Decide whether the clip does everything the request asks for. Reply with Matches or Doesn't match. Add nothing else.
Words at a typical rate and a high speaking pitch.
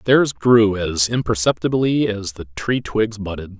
Doesn't match